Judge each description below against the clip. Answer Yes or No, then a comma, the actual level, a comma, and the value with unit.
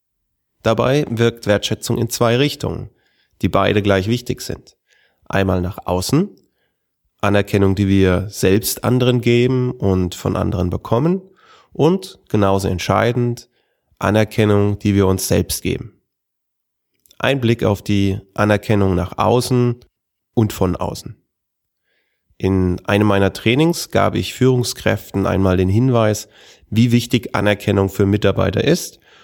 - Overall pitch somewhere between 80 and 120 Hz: Yes, low, 105 Hz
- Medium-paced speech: No, slow, 120 wpm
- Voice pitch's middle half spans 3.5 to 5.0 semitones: Yes, average, 3.8 semitones